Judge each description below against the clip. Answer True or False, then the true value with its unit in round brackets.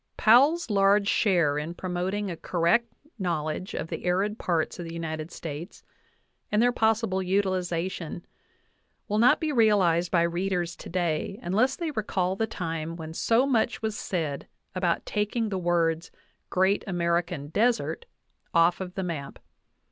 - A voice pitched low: False (185 Hz)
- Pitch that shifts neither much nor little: True (3.8 semitones)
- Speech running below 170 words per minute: True (150 wpm)